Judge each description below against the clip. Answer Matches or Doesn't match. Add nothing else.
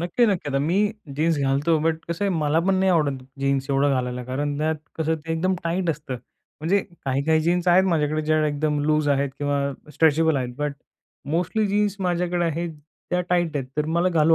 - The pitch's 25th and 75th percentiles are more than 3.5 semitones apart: Doesn't match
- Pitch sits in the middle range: Matches